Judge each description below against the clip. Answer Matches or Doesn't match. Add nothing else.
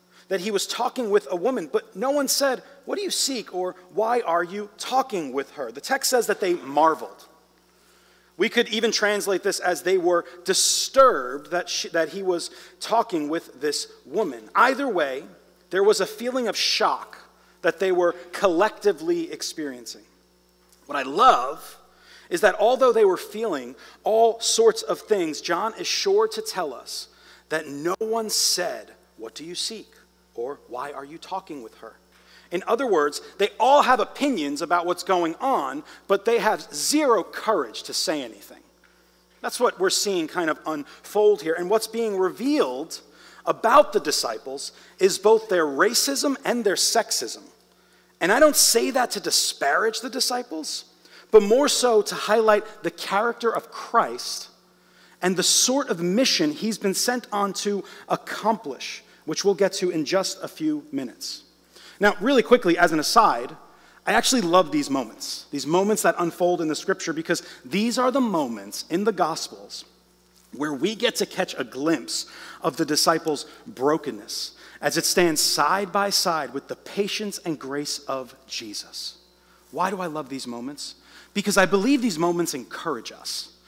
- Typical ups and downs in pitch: Doesn't match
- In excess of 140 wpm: Matches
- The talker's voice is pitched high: Matches